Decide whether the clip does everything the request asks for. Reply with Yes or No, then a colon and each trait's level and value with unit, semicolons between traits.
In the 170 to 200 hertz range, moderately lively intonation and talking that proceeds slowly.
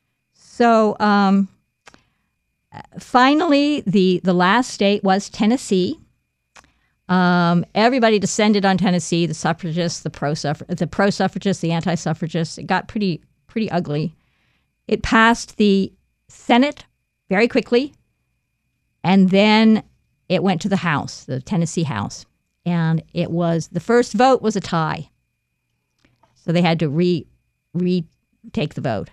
Yes: medium, 185 Hz; average, 4.4 semitones; slow, 125 wpm